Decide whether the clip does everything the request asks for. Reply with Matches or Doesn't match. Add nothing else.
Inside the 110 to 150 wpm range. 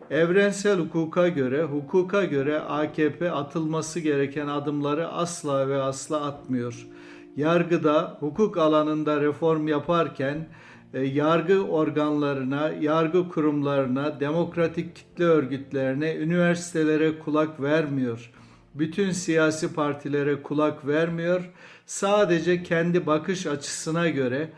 Doesn't match